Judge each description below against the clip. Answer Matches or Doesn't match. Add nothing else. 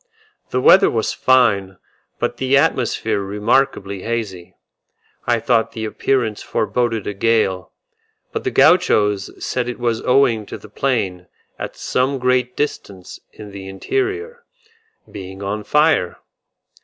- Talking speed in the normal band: Doesn't match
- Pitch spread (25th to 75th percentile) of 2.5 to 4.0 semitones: Doesn't match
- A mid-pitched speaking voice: Doesn't match